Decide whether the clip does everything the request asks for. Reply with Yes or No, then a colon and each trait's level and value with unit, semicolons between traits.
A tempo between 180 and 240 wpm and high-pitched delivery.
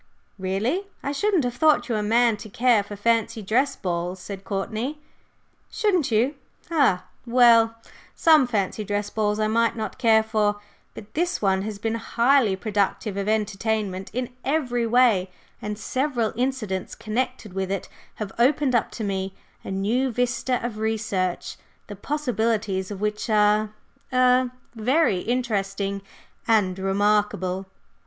No: average, 145 wpm; high, 220 Hz